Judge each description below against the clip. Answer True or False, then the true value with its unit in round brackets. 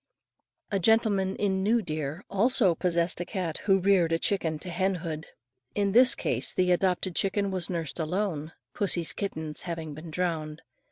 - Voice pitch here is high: False (180 Hz)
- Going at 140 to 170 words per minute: True (165 wpm)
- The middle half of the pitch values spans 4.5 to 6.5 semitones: False (3.3 semitones)